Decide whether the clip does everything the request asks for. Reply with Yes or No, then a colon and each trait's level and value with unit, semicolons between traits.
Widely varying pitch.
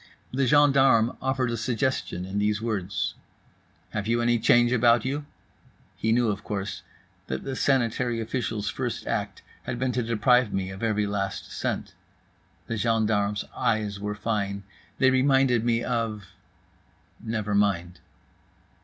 No: average, 3.0 semitones